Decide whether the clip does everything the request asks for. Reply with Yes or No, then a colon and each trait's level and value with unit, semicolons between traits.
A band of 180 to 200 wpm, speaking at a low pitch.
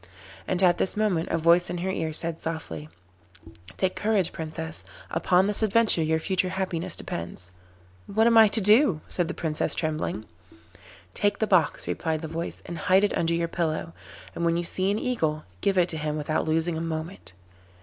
No: average, 190 wpm; medium, 170 Hz